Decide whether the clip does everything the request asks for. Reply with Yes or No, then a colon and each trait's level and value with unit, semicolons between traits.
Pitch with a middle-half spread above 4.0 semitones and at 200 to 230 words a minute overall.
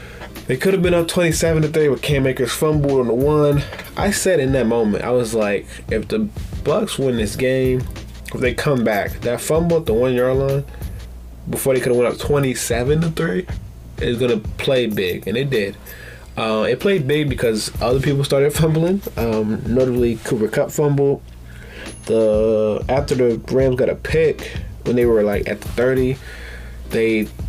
No: average, 5.1 semitones; average, 185 wpm